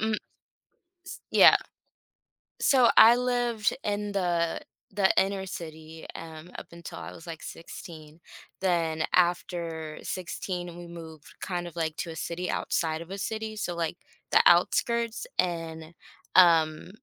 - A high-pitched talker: No, medium, 175 Hz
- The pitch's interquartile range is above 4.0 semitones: No, average, 3.2 semitones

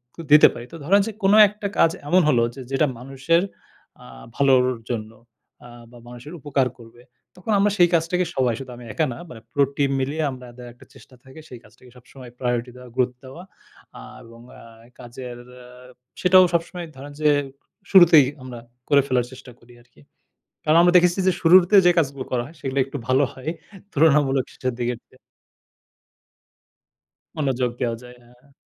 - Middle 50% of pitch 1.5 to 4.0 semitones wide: No, average, 4.5 semitones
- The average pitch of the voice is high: No, low, 135 Hz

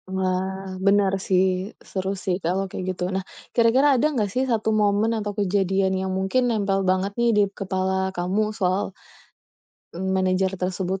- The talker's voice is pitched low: No, high, 190 Hz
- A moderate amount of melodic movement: No, narrow, 1.6 semitones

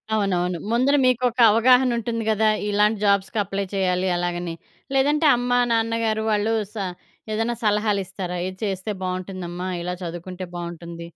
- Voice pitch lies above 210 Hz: No, high, 200 Hz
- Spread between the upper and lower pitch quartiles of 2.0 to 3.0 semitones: No, average, 3.9 semitones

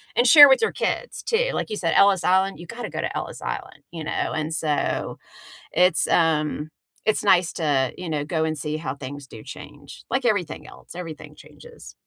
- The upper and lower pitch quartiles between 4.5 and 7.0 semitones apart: Yes, average, 5.1 semitones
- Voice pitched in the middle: Yes, medium, 165 Hz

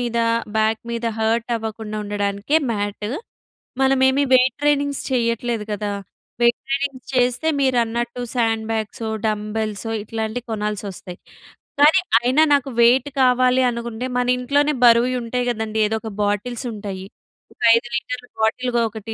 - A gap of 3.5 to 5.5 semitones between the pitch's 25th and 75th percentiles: No, narrow, 2.4 semitones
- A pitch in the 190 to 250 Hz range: Yes, high, 235 Hz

